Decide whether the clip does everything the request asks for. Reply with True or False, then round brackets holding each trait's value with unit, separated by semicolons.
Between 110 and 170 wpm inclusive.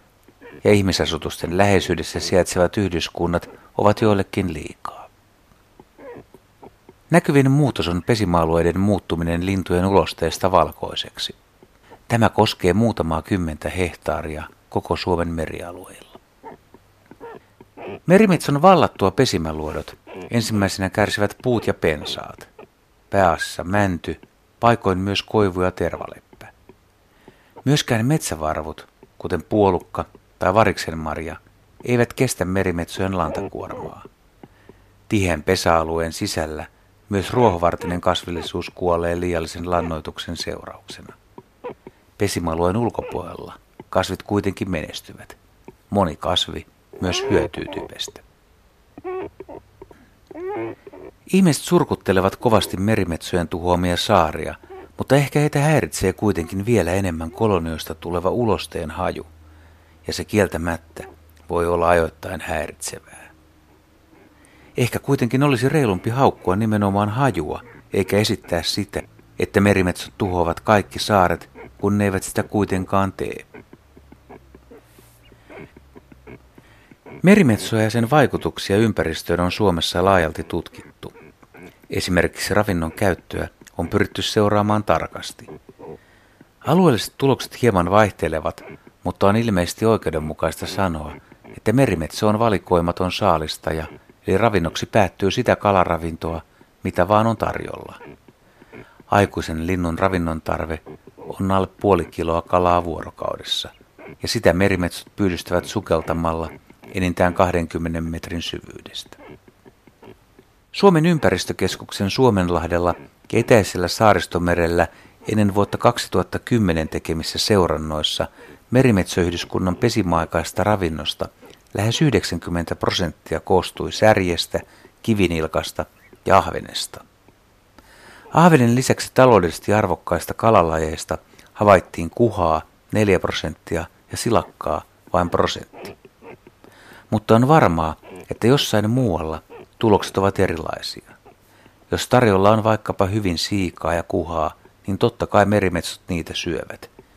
False (95 wpm)